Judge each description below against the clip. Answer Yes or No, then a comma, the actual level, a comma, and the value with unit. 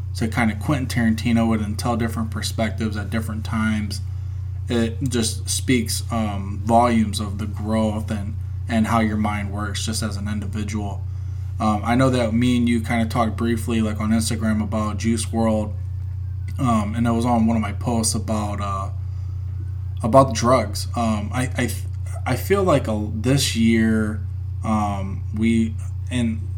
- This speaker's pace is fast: No, average, 165 wpm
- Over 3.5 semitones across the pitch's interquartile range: No, average, 2.9 semitones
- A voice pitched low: Yes, low, 105 Hz